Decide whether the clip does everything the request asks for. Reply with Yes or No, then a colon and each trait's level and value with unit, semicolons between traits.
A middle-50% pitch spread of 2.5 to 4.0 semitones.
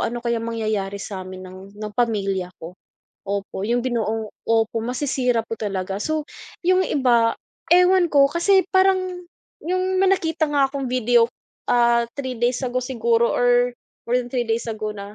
No: average, 4.4 semitones